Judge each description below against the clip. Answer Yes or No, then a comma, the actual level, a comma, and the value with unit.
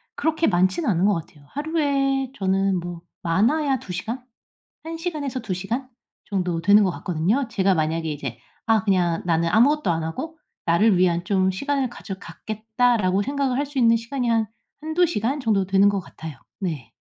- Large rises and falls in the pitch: Yes, wide, 7.1 semitones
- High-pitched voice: Yes, high, 205 Hz